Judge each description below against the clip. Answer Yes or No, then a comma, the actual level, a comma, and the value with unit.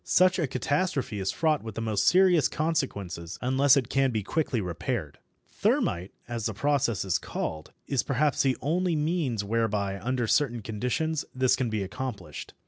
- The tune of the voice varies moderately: No, wide, 6.1 semitones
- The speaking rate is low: No, average, 165 wpm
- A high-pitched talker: No, low, 125 Hz